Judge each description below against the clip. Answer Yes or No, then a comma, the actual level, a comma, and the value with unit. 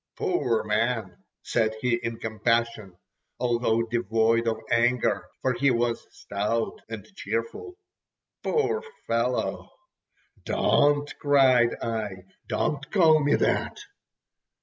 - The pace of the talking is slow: Yes, slow, 100 wpm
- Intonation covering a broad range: No, average, 3.2 semitones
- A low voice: Yes, low, 115 Hz